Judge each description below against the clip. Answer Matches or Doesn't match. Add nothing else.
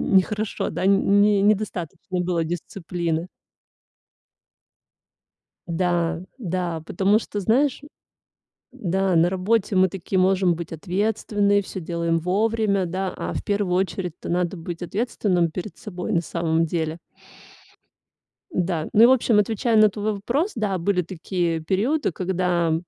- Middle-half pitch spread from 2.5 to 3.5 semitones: Matches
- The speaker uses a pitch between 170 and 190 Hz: Matches